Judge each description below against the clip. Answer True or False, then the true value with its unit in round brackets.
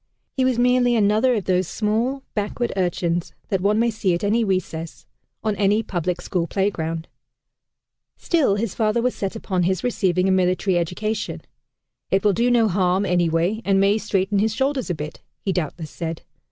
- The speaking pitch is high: True (195 Hz)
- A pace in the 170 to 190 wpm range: True (175 wpm)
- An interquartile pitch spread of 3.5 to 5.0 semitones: True (3.8 semitones)